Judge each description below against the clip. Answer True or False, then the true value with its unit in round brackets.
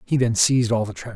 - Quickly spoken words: True (310 wpm)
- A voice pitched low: True (120 Hz)